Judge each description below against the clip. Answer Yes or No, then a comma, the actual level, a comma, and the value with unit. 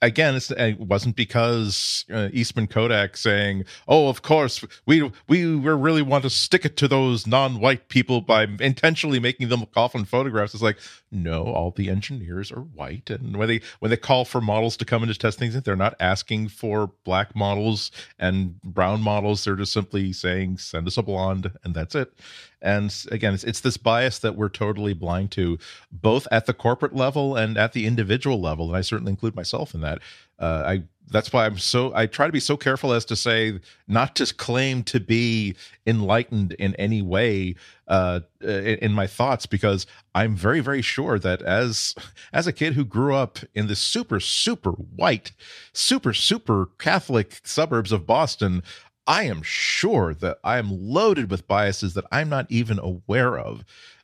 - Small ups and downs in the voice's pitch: No, average, 4.4 semitones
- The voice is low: Yes, low, 110 Hz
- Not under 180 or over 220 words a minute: Yes, average, 185 wpm